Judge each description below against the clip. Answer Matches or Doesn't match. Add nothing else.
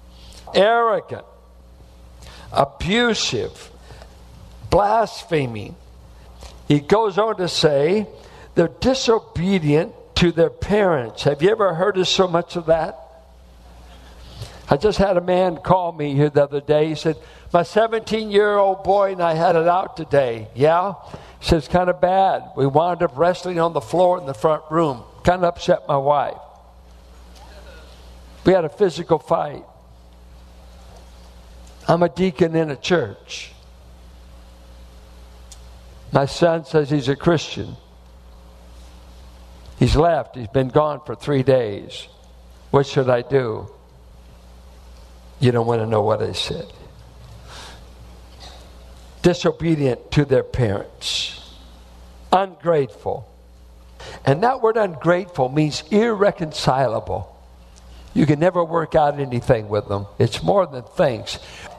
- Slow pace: Matches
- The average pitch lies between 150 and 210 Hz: Doesn't match